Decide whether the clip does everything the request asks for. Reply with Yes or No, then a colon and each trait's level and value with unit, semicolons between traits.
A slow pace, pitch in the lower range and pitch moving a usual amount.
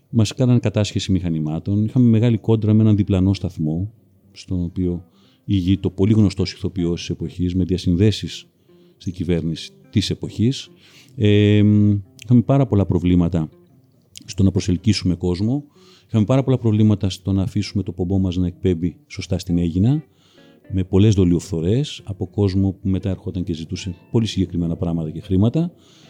No: average, 145 wpm; very low, 95 Hz; average, 3.5 semitones